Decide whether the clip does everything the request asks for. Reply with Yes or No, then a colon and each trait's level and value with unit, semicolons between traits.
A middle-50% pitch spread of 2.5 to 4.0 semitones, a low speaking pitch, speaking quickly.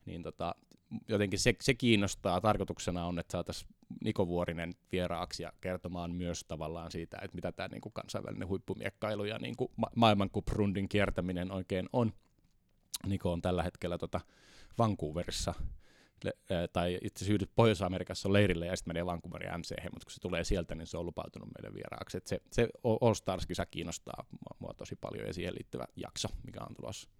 Yes: average, 2.9 semitones; very low, 90 Hz; fast, 170 wpm